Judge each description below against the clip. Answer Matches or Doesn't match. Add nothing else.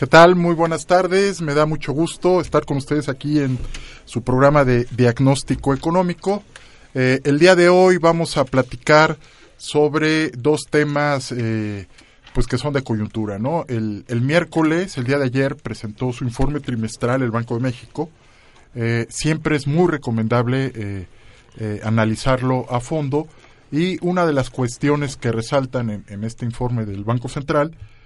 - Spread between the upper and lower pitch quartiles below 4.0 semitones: Doesn't match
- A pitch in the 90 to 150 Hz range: Matches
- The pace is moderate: Matches